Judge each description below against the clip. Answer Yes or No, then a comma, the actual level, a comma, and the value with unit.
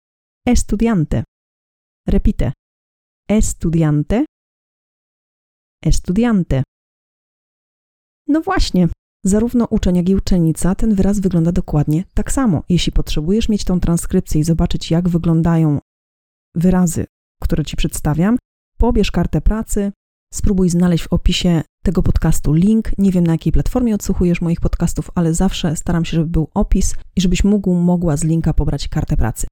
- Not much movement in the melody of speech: No, average, 3.7 semitones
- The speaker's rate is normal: Yes, average, 130 wpm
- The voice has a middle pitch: Yes, medium, 175 Hz